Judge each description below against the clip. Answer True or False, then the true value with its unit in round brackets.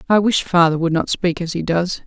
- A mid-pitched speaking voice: True (175 Hz)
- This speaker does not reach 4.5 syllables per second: False (5.3 syllables/s)